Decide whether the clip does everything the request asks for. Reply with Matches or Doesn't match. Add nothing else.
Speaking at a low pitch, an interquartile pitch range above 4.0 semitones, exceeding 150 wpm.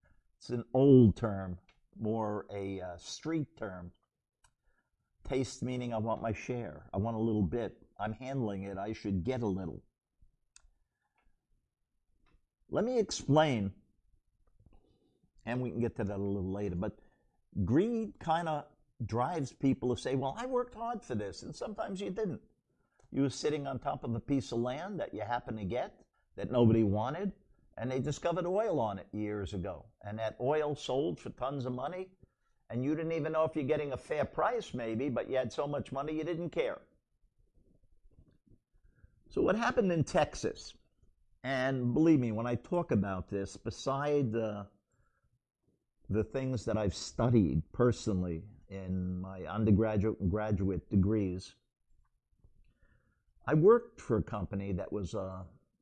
Matches